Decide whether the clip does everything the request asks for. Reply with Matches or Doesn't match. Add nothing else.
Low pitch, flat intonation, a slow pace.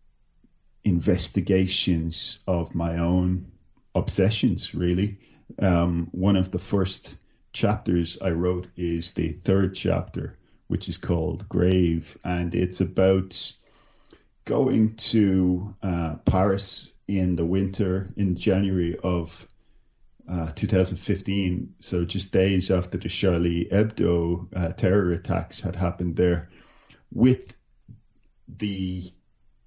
Matches